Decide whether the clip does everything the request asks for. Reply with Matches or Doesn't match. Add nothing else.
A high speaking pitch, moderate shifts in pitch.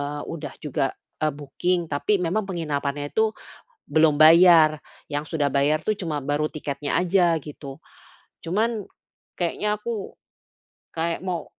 Doesn't match